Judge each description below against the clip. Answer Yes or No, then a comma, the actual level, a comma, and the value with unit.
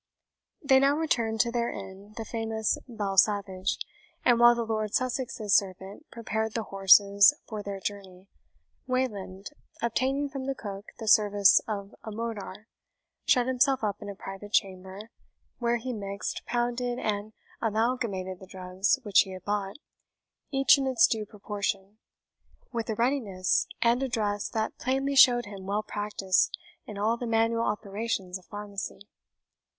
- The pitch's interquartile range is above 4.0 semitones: No, average, 3.2 semitones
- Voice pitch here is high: Yes, high, 215 Hz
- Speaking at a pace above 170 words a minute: No, average, 150 wpm